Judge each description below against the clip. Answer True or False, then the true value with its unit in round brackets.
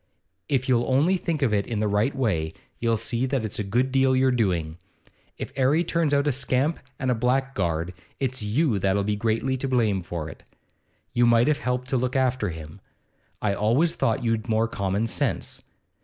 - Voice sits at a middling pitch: False (120 Hz)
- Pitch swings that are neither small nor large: True (4.2 semitones)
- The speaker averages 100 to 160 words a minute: False (195 wpm)